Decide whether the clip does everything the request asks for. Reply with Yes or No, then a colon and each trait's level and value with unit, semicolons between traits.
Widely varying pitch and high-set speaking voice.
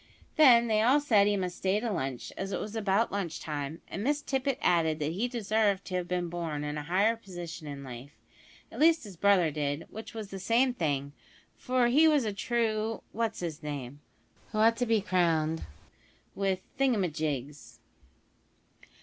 Yes: wide, 6.3 semitones; high, 195 Hz